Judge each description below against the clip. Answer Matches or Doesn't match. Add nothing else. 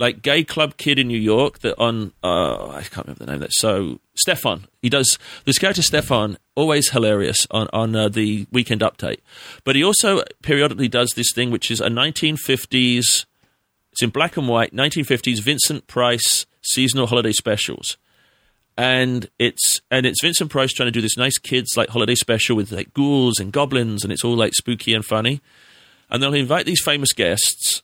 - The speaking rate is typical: Matches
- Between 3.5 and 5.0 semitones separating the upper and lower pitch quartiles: Matches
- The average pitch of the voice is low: Matches